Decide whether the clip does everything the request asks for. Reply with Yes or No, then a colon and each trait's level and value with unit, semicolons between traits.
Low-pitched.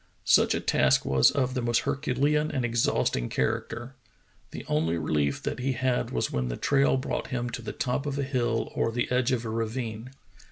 Yes: low, 120 Hz